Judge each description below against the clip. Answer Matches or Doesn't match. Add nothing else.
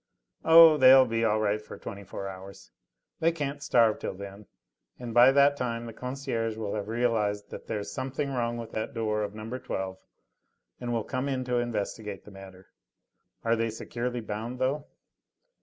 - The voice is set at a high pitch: Doesn't match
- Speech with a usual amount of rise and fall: Matches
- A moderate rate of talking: Matches